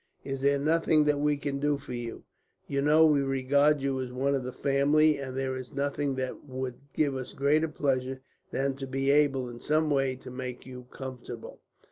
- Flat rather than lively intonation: Yes, narrow, 1.9 semitones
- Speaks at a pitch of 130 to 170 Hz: Yes, low, 135 Hz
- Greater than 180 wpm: Yes, average, 200 wpm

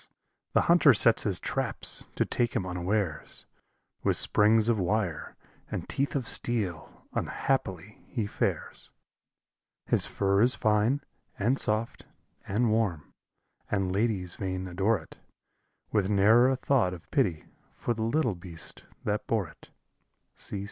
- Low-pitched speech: Yes, low, 105 Hz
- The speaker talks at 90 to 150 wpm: Yes, slow, 135 wpm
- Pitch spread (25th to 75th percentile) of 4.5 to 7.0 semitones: No, average, 3.9 semitones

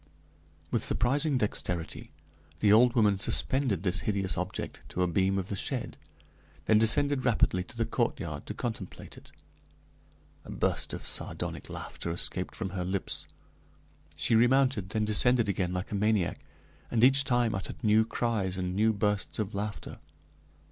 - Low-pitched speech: Yes, low, 105 Hz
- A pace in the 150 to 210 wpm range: Yes, average, 155 wpm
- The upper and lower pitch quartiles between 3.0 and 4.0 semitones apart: Yes, average, 3.7 semitones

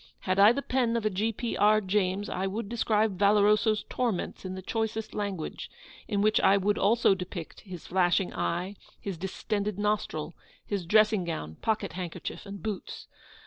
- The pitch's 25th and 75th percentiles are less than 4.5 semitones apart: Yes, narrow, 2.5 semitones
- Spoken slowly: No, average, 170 wpm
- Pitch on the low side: No, high, 205 Hz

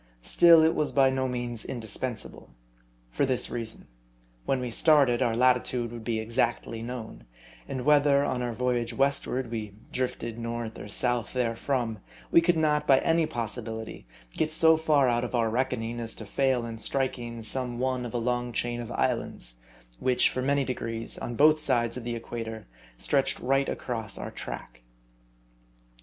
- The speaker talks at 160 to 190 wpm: Yes, average, 165 wpm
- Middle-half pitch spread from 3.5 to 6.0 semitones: No, narrow, 2.5 semitones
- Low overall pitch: Yes, low, 120 Hz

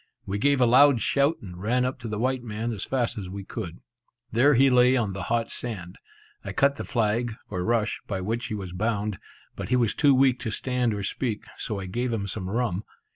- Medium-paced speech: No, fast, 230 wpm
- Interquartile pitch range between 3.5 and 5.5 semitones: Yes, average, 3.8 semitones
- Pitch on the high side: No, low, 115 Hz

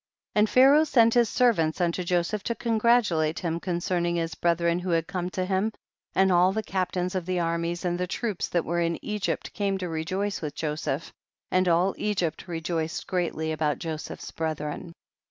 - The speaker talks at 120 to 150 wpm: No, average, 175 wpm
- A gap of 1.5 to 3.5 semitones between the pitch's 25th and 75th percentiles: Yes, average, 2.8 semitones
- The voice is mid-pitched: Yes, medium, 175 Hz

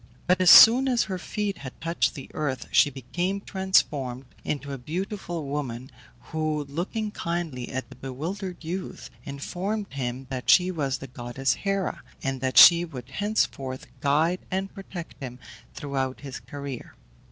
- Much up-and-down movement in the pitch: Yes, wide, 5.7 semitones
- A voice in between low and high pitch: Yes, medium, 150 Hz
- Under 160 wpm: Yes, average, 150 wpm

